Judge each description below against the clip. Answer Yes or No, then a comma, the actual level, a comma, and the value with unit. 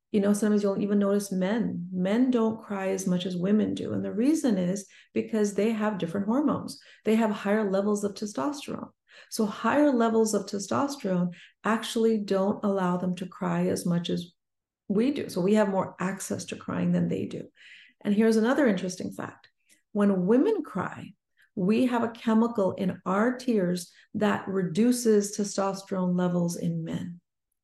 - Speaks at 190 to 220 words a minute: No, average, 165 wpm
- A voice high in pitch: Yes, high, 205 Hz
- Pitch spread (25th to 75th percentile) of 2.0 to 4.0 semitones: Yes, average, 3.1 semitones